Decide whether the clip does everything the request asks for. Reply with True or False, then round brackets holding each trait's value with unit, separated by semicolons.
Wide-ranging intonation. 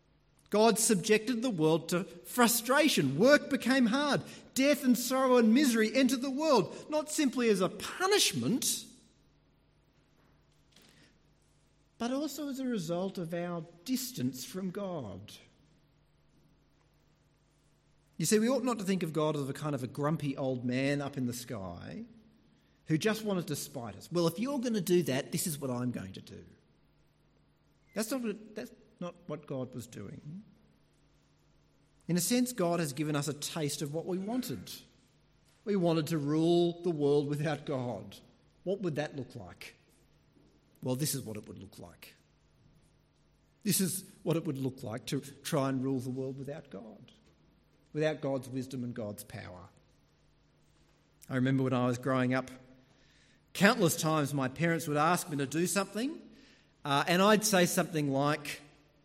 True (7.9 semitones)